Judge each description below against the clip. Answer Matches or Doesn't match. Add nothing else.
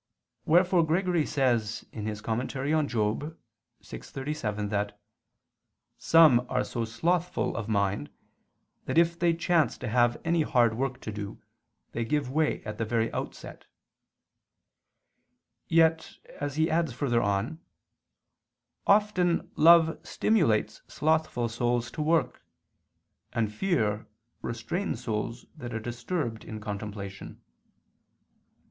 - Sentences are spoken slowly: Matches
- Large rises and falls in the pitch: Matches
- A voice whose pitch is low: Matches